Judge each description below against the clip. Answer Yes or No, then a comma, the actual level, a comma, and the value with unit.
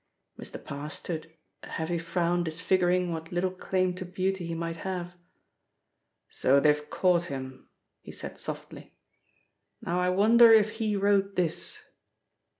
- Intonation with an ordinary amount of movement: No, narrow, 2.3 semitones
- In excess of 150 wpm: No, average, 140 wpm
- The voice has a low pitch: No, medium, 175 Hz